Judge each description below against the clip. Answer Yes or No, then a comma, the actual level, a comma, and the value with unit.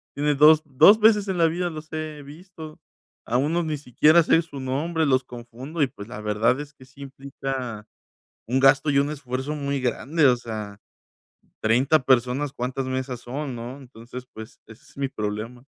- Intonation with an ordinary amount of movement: Yes, average, 3.6 semitones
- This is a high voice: No, low, 135 Hz